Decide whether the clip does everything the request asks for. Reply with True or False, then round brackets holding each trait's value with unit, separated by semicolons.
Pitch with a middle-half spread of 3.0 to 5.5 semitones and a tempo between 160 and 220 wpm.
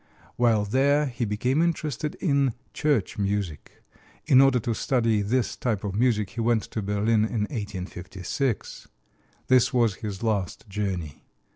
False (4.0 semitones; 140 wpm)